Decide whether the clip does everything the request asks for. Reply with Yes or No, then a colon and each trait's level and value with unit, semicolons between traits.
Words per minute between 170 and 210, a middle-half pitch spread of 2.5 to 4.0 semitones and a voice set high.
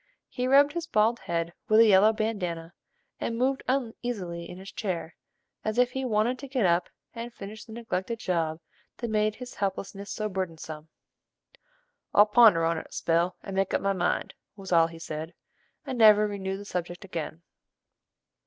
No: average, 175 wpm; average, 5.0 semitones; high, 200 Hz